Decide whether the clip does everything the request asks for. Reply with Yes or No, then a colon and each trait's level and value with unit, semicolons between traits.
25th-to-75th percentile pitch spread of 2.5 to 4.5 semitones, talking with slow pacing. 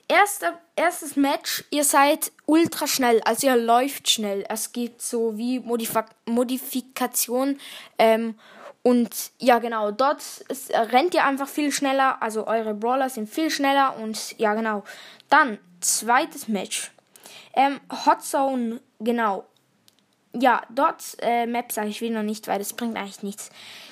No: average, 4.1 semitones; average, 145 wpm